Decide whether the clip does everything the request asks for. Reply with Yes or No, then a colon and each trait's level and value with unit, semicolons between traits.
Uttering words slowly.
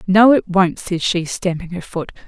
No: fast, 210 wpm